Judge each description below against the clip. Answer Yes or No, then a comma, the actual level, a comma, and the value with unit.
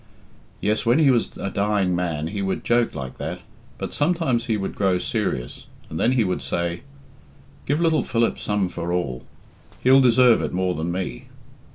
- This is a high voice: No, low, 100 Hz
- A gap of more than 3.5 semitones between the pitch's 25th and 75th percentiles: Yes, wide, 5.5 semitones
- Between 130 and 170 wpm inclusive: No, average, 180 wpm